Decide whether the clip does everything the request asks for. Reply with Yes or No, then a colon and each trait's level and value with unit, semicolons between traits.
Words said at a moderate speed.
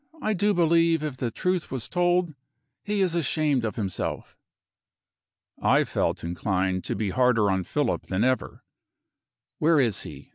Yes: average, 150 wpm